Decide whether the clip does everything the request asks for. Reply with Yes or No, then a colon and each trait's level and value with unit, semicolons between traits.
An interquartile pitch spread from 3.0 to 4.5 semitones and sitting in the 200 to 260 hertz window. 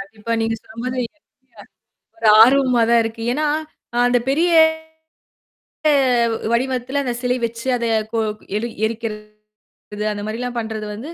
No: narrow, 2.5 semitones; high, 235 Hz